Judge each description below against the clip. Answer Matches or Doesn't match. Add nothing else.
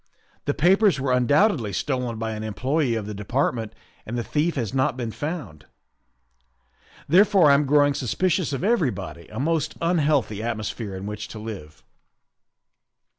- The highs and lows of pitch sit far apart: Matches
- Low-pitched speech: Matches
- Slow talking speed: Doesn't match